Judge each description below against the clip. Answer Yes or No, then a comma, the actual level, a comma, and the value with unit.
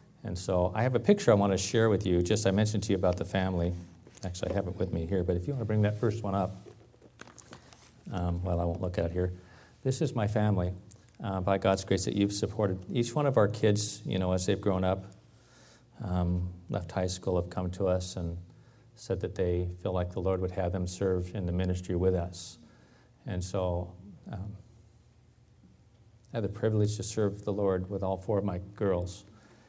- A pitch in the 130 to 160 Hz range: No, very low, 95 Hz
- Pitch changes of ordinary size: Yes, average, 3.1 semitones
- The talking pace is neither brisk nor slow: No, fast, 220 wpm